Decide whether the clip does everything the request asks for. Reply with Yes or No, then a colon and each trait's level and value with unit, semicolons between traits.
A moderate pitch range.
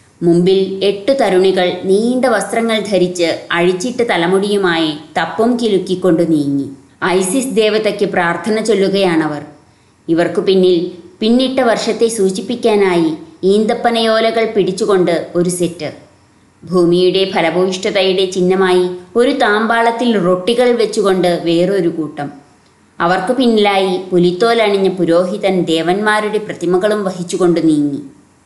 Yes: average, 3.8 semitones